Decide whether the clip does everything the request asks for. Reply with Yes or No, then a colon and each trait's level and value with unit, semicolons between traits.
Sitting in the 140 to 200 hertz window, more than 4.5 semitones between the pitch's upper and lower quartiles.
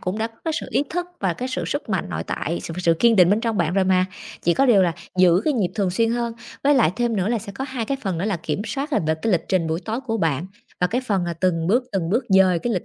Yes: high, 195 Hz; average, 5.0 semitones